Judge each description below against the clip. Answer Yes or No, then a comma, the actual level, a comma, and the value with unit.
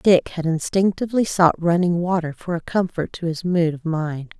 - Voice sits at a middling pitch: Yes, medium, 170 Hz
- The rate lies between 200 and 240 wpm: No, average, 190 wpm